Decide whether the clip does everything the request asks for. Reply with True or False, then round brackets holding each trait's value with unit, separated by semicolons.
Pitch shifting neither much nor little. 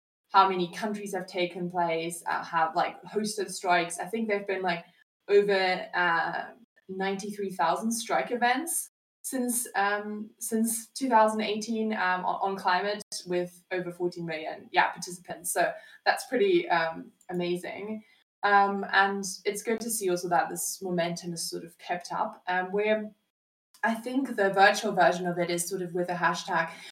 True (3.3 semitones)